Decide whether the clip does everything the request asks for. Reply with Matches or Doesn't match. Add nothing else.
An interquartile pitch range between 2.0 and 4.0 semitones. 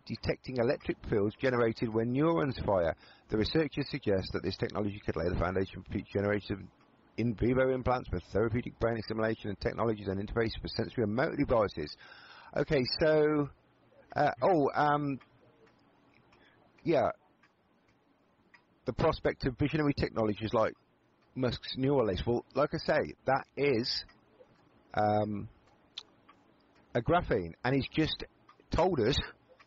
Doesn't match